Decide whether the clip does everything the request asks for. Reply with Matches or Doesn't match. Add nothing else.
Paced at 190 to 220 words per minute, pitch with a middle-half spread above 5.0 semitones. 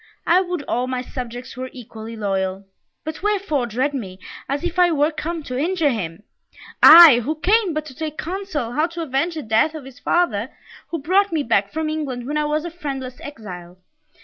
Matches